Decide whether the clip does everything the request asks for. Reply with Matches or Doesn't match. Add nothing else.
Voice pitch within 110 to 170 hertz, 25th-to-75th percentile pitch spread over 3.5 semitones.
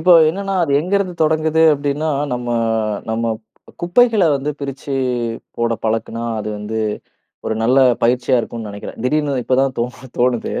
Matches